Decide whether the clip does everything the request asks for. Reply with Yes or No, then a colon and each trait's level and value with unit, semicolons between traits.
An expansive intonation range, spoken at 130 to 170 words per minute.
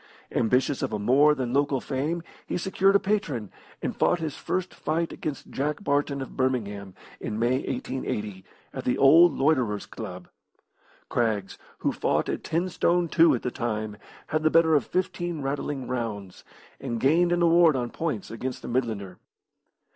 Yes: wide, 5.7 semitones; average, 165 wpm